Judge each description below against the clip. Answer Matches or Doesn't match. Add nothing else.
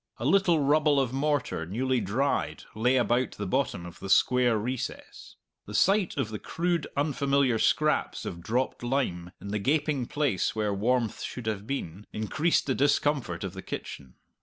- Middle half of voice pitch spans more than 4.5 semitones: Matches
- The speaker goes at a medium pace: Matches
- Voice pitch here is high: Doesn't match